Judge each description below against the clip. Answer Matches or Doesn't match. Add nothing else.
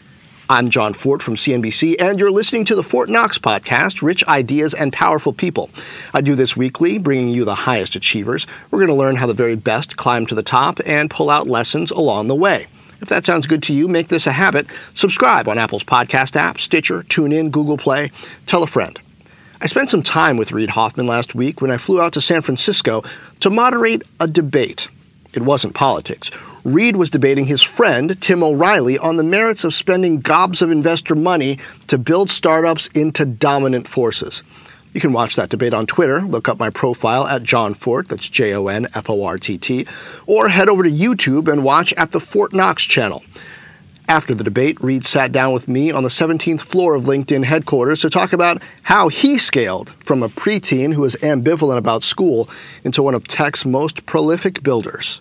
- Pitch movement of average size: Matches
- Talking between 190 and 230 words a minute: Matches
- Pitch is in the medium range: Matches